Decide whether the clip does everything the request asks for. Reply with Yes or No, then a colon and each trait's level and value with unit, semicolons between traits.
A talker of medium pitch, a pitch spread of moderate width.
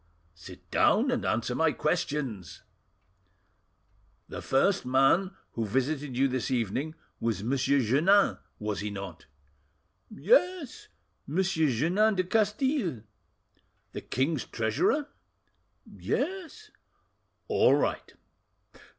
No: medium, 145 Hz; wide, 8.6 semitones